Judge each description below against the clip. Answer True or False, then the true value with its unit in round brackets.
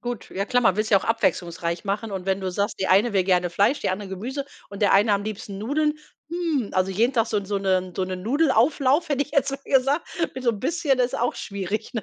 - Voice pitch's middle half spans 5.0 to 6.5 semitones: True (5.5 semitones)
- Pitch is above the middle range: True (215 Hz)